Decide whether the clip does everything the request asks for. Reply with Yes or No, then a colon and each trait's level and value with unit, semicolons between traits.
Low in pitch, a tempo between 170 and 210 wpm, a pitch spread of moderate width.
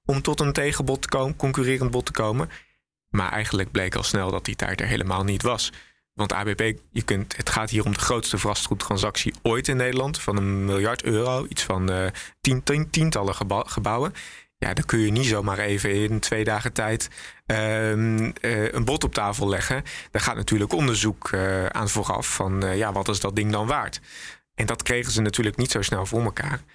Yes: low, 110 Hz; fast, 200 wpm; average, 3.6 semitones